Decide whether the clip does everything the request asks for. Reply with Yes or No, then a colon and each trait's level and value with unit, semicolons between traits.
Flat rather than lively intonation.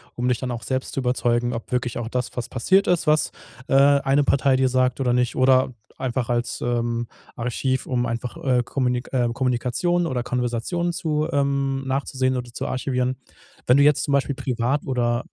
Yes: narrow, 2.0 semitones